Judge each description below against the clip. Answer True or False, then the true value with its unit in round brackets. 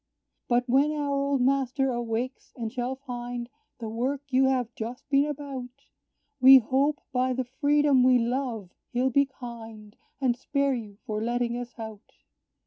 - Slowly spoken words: False (155 wpm)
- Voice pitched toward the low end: False (255 Hz)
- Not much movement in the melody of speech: True (2.3 semitones)